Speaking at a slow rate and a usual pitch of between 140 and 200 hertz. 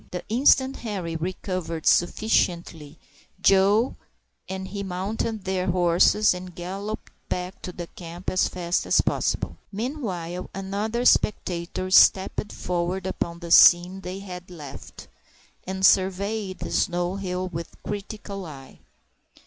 Yes: slow, 125 wpm; medium, 185 Hz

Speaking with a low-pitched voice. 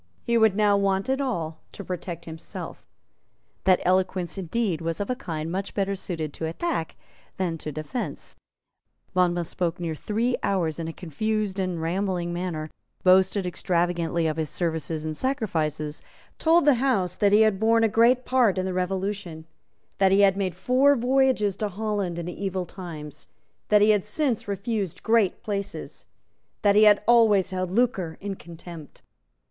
No: high, 190 Hz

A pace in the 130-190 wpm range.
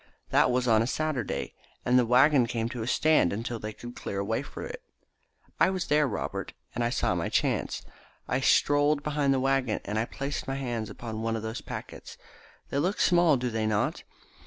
No: fast, 205 wpm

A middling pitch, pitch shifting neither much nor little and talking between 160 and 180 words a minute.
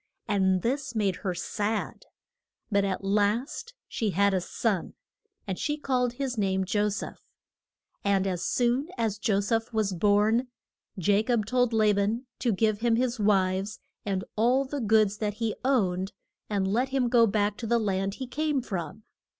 No: high, 215 Hz; average, 3.3 semitones; average, 170 wpm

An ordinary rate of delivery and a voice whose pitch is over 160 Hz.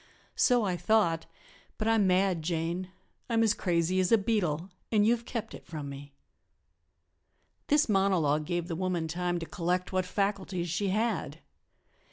Yes: average, 160 wpm; medium, 185 Hz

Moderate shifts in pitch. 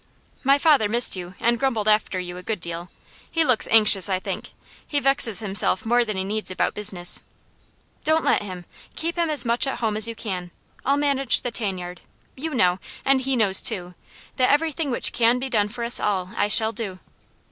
No: wide, 5.7 semitones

